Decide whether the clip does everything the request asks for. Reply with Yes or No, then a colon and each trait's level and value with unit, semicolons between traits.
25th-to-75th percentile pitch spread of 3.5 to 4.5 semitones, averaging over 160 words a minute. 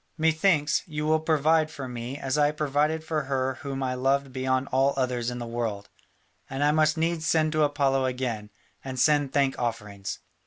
No: average, 3.1 semitones; average, 185 wpm